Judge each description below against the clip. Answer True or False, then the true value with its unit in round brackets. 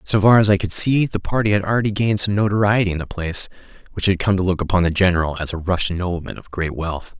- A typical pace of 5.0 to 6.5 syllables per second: False (6.8 syllables/s)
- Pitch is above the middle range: False (95 Hz)